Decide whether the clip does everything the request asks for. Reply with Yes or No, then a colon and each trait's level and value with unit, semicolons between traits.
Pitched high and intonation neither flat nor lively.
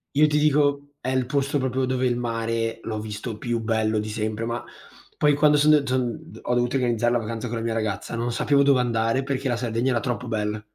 No: low, 120 Hz; average, 3.0 semitones